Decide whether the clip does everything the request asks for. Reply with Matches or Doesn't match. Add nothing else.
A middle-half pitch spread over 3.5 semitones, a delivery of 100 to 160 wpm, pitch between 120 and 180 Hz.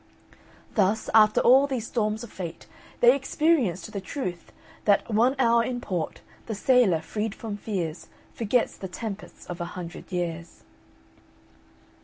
Doesn't match